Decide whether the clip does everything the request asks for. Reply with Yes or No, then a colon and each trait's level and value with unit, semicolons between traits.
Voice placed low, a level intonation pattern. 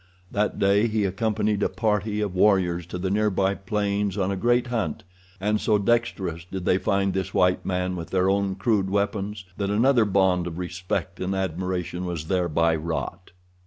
Yes: very low, 95 Hz; narrow, 2.3 semitones